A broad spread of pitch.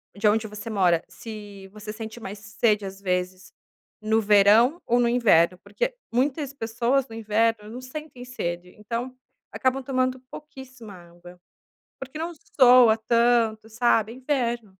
No: average, 3.5 semitones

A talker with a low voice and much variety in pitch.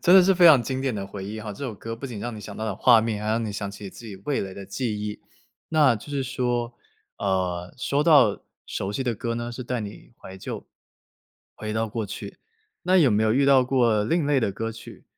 No: low, 115 Hz; average, 4.0 semitones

